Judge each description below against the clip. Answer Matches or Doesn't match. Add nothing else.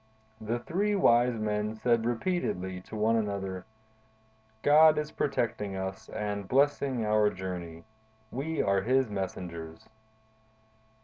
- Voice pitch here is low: Matches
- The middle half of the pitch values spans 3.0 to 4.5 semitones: Doesn't match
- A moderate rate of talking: Doesn't match